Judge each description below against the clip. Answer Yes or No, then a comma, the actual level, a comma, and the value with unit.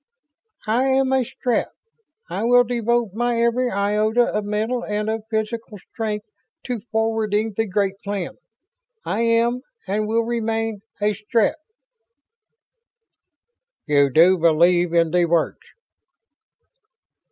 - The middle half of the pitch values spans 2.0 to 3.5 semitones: Yes, narrow, 2.6 semitones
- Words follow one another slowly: Yes, slow, 120 wpm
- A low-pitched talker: No, high, 220 Hz